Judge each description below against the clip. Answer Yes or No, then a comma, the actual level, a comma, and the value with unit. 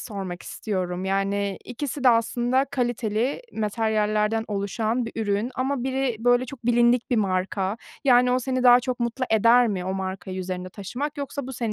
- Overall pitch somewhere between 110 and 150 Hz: No, high, 230 Hz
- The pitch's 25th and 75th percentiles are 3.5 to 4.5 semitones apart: Yes, average, 3.9 semitones